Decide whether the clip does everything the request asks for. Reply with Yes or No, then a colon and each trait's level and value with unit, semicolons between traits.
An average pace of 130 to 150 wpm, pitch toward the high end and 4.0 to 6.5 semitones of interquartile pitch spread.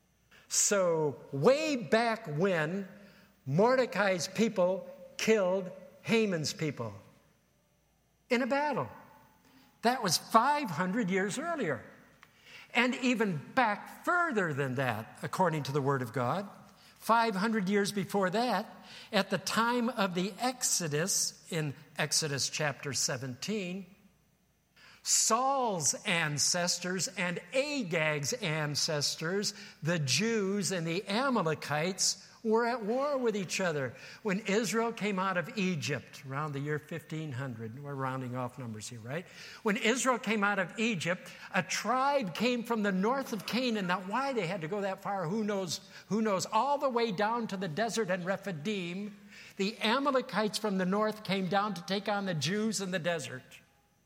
Yes: average, 140 wpm; high, 195 Hz; average, 5.1 semitones